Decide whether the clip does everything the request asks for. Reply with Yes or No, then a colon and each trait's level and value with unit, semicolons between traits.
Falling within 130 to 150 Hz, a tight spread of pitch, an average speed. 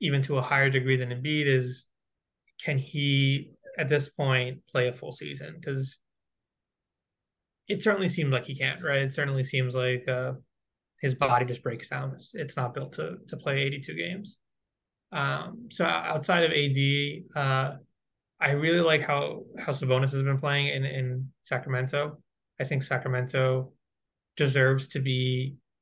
Yes: low, 135 Hz; narrow, 2.0 semitones; average, 160 wpm